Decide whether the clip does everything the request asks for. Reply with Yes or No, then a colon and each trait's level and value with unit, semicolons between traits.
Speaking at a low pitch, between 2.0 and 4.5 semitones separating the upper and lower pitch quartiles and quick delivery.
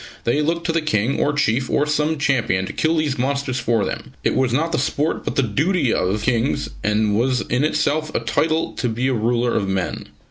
No: low, 130 Hz; average, 4.9 semitones; fast, 220 wpm